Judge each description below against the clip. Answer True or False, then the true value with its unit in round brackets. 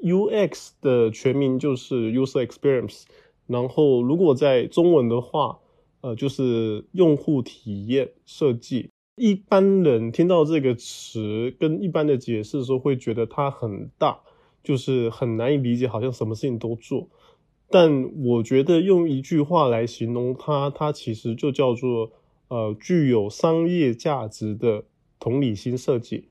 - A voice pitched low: True (130 Hz)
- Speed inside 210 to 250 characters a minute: True (245 characters per minute)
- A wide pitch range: False (4.5 semitones)